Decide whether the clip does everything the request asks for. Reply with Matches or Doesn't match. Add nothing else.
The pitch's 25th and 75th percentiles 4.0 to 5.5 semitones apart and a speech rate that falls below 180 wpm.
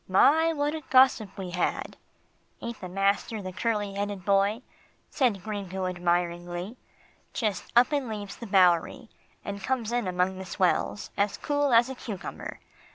Matches